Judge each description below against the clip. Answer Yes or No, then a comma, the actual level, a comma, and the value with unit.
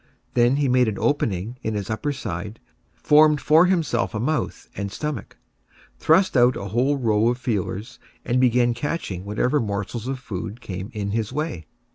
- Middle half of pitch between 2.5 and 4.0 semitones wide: No, average, 5.2 semitones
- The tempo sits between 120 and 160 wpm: No, average, 170 wpm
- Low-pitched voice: Yes, low, 120 Hz